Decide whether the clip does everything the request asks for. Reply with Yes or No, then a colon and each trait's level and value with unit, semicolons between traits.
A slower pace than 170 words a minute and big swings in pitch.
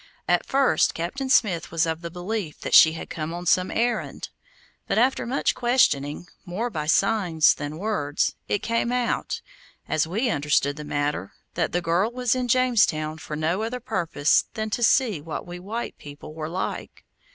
No: average, 175 wpm; wide, 6.8 semitones